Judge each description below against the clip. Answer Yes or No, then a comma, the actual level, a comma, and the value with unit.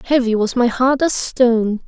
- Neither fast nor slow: Yes, average, 190 wpm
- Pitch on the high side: Yes, high, 245 Hz